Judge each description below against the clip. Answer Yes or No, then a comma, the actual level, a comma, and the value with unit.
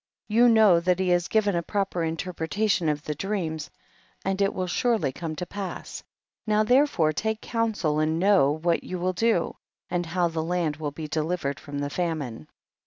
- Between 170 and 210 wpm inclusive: Yes, average, 185 wpm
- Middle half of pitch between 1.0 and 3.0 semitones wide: No, average, 4.2 semitones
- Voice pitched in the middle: Yes, medium, 175 Hz